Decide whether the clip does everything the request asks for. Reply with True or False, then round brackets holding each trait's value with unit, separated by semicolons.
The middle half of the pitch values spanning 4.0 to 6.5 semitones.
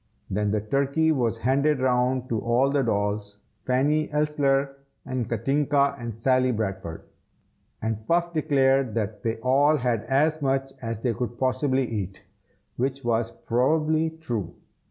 False (3.6 semitones)